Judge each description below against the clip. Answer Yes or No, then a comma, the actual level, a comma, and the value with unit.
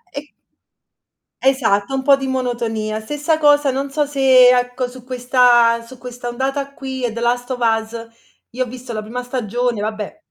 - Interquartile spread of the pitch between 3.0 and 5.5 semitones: No, narrow, 2.4 semitones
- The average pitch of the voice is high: Yes, very high, 250 Hz